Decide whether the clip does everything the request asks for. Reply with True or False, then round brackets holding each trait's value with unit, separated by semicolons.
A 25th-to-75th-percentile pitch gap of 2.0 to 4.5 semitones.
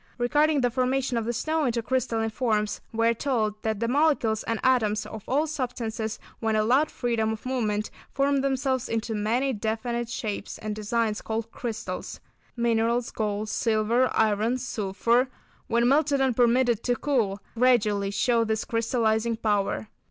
True (2.7 semitones)